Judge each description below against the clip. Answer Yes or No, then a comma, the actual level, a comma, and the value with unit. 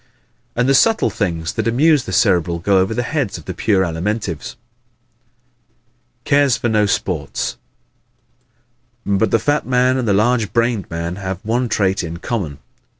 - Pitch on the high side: No, low, 105 Hz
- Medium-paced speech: Yes, average, 160 wpm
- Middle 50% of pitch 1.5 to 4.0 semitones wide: No, average, 5.2 semitones